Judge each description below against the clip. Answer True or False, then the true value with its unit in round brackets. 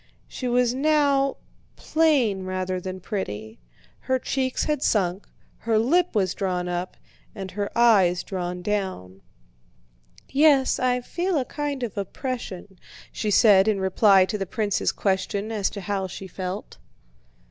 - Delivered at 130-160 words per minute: True (140 wpm)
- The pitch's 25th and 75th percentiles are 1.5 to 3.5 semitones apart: False (5.4 semitones)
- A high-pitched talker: True (205 Hz)